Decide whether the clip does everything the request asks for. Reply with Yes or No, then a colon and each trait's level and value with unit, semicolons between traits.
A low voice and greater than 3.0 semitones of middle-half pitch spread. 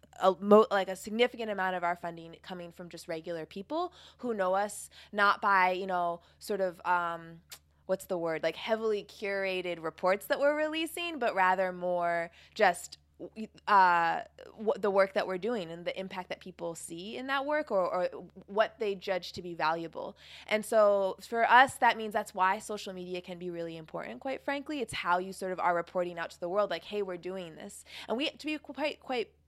No: high, 190 Hz; average, 3.6 semitones